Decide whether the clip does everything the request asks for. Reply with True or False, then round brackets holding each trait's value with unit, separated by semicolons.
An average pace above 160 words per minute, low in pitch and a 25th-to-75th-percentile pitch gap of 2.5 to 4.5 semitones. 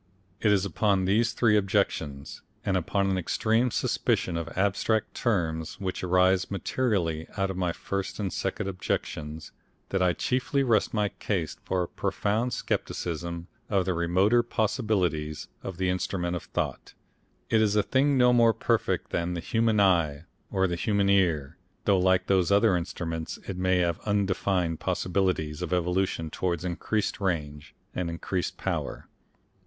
False (155 wpm; 95 Hz; 3.1 semitones)